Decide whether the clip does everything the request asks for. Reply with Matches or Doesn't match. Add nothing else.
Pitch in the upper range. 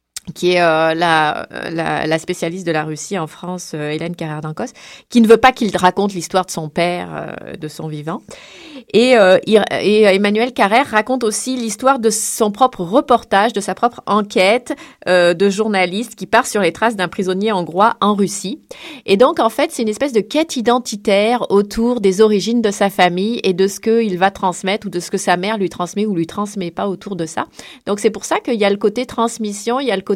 Matches